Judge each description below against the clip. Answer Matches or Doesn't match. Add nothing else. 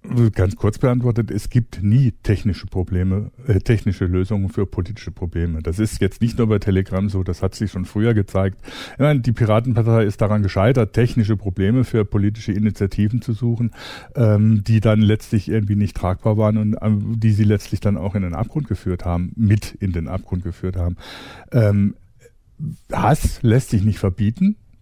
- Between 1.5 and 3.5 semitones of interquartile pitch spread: Matches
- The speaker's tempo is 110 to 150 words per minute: Doesn't match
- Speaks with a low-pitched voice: Matches